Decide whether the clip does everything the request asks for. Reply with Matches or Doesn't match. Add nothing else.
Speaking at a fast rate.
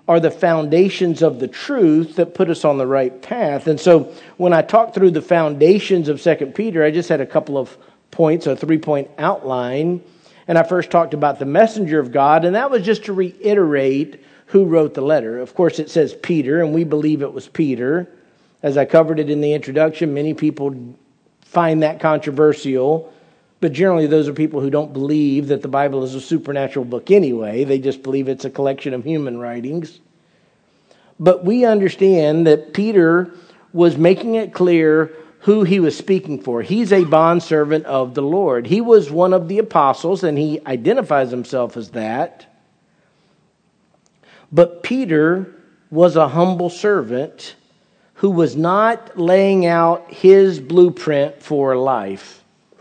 Doesn't match